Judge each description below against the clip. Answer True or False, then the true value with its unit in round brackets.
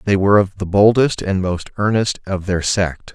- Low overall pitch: True (95 Hz)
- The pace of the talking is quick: True (210 wpm)